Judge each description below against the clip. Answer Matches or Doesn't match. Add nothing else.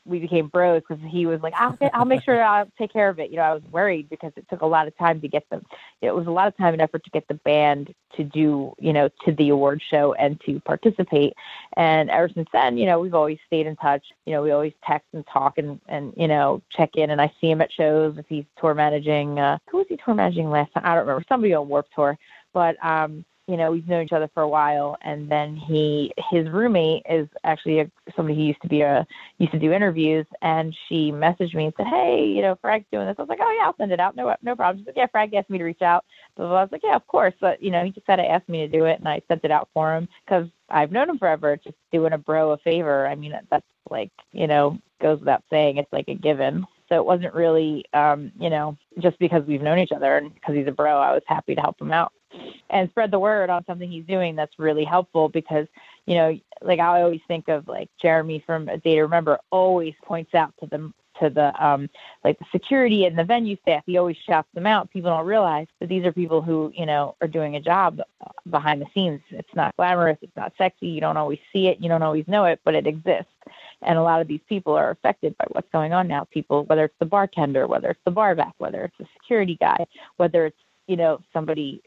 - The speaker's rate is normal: Doesn't match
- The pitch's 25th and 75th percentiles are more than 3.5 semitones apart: Doesn't match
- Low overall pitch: Doesn't match